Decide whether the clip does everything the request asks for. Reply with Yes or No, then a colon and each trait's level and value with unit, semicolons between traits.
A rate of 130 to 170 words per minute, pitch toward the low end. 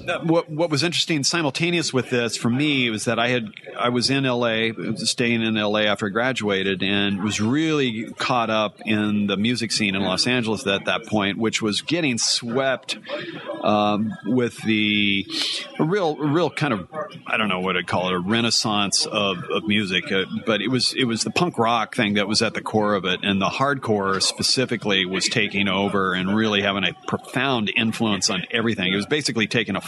No: average, 200 wpm; low, 110 Hz